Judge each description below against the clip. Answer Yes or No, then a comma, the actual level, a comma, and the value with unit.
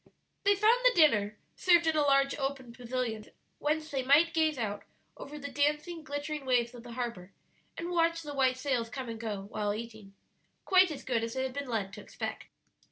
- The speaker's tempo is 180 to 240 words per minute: Yes, average, 200 wpm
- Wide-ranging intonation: No, average, 5.0 semitones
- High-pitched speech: Yes, very high, 270 Hz